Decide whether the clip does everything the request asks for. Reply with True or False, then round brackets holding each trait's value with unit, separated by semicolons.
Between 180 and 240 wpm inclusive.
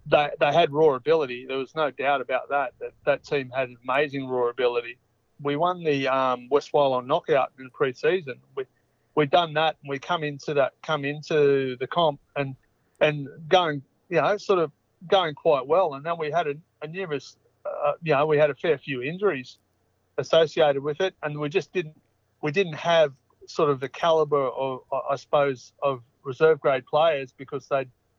True (190 wpm)